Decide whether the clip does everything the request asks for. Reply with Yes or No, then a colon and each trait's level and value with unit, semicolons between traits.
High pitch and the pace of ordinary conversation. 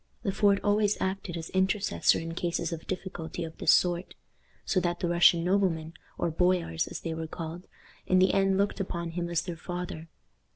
No: medium, 175 Hz; average, 190 wpm